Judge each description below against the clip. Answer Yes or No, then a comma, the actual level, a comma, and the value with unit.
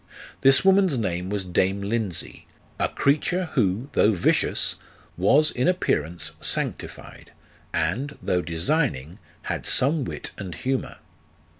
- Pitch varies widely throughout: Yes, wide, 8.1 semitones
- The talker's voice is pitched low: Yes, low, 110 Hz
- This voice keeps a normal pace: No, slow, 120 wpm